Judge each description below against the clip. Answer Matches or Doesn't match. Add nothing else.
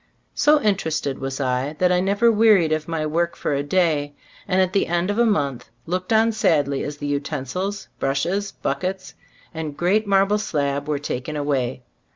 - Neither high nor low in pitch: Matches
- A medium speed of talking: Matches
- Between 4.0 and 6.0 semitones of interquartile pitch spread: Matches